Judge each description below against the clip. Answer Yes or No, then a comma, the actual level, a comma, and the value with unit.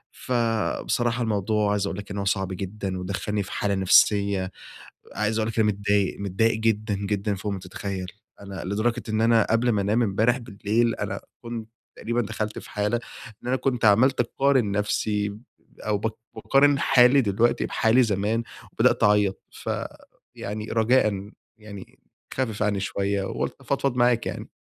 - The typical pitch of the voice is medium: No, low, 105 Hz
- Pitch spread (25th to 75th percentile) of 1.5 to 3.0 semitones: Yes, narrow, 2.6 semitones